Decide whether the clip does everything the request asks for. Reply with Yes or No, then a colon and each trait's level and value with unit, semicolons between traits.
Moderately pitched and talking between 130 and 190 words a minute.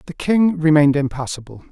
Yes: medium, 155 Hz; average, 140 wpm